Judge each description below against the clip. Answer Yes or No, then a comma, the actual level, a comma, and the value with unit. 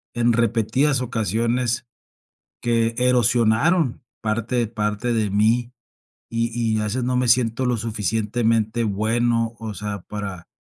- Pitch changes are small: Yes, narrow, 2.0 semitones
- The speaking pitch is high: No, low, 115 Hz